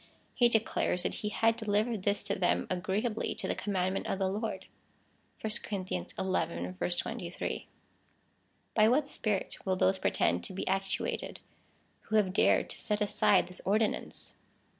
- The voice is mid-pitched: No, high, 200 Hz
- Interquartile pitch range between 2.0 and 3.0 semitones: Yes, average, 2.7 semitones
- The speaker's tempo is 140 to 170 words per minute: Yes, average, 145 wpm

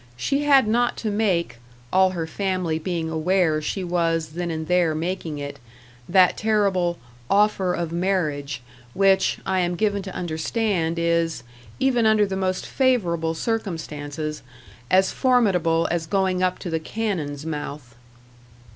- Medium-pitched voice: Yes, medium, 180 Hz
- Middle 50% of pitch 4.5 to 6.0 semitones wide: No, average, 3.5 semitones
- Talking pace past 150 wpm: No, average, 140 wpm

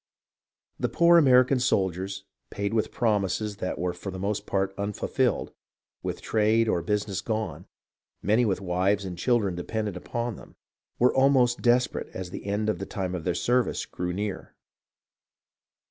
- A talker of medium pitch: No, low, 105 Hz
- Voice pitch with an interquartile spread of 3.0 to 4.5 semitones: Yes, average, 3.8 semitones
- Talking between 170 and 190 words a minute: No, average, 160 wpm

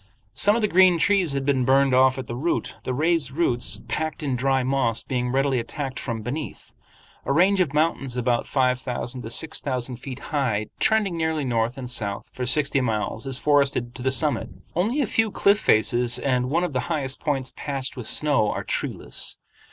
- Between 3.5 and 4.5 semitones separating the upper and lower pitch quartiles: Yes, average, 3.8 semitones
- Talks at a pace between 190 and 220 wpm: Yes, average, 200 wpm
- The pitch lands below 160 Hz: Yes, low, 135 Hz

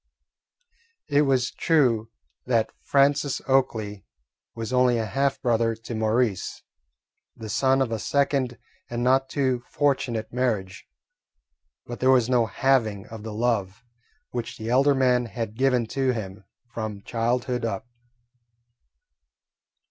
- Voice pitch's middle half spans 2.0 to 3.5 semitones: Yes, average, 2.9 semitones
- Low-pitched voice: Yes, low, 120 Hz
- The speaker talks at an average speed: No, slow, 125 wpm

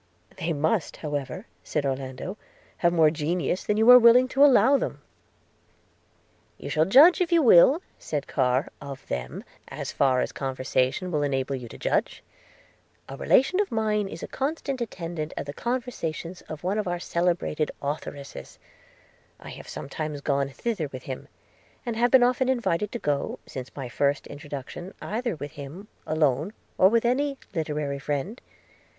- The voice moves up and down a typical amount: No, wide, 8.4 semitones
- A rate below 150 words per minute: No, average, 165 wpm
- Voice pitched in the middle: Yes, medium, 165 Hz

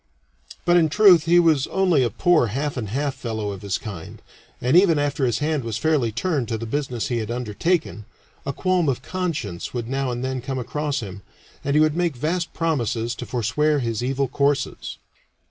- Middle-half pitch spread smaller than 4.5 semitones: No, average, 5.1 semitones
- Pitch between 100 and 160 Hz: Yes, low, 135 Hz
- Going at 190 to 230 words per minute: Yes, average, 195 wpm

